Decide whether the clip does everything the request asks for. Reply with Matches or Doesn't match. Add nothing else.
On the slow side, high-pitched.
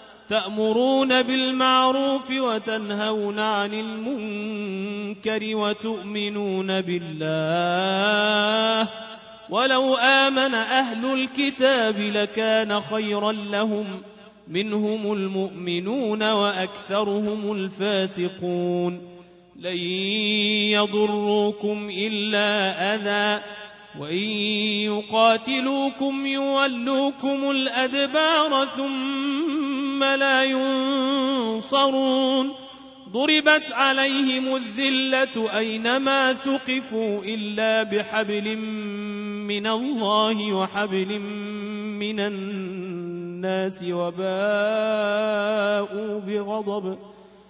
Matches